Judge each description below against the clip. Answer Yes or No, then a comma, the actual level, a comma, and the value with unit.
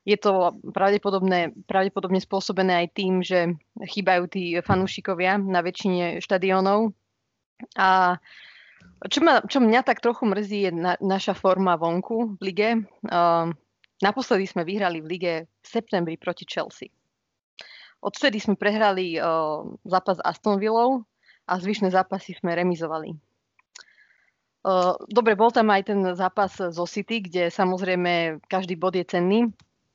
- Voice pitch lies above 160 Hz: Yes, high, 190 Hz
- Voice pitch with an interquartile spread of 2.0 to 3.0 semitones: Yes, average, 2.7 semitones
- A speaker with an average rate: Yes, average, 135 wpm